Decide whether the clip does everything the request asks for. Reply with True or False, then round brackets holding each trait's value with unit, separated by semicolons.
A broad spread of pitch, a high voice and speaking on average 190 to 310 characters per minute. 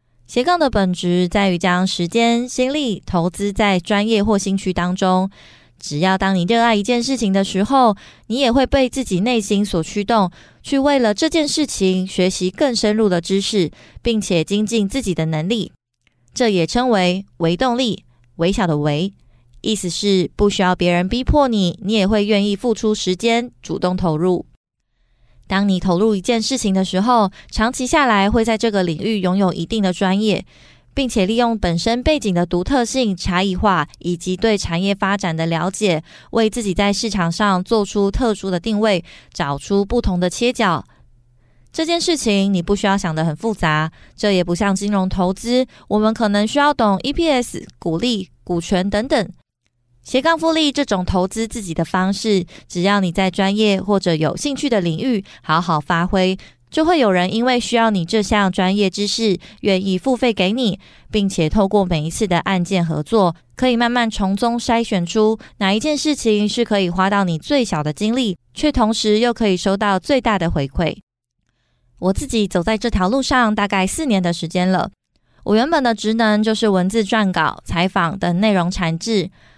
False (4.1 semitones; 200 Hz; 265 characters per minute)